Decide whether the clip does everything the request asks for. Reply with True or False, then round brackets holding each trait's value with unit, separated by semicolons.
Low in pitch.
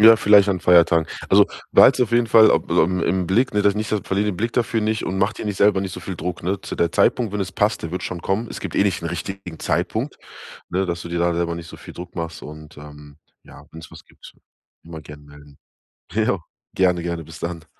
True (90 Hz)